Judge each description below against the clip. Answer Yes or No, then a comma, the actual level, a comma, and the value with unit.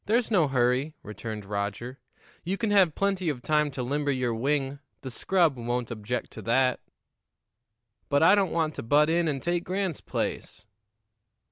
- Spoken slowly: No, average, 165 wpm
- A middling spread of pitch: No, wide, 5.8 semitones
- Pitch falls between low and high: Yes, medium, 145 Hz